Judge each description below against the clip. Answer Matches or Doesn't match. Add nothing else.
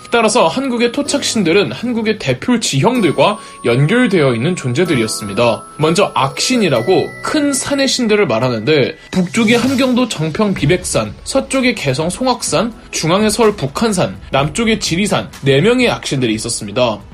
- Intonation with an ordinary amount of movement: Doesn't match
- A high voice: Matches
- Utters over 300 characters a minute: Matches